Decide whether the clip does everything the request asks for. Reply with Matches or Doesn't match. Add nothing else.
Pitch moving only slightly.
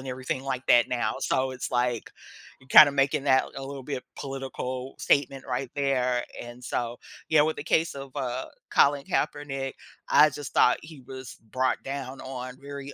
Matches